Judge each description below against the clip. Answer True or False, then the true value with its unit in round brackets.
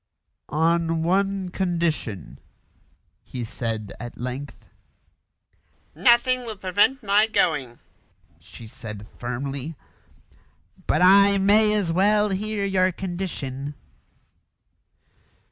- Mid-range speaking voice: True (175 Hz)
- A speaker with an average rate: False (90 wpm)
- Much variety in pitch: True (7.2 semitones)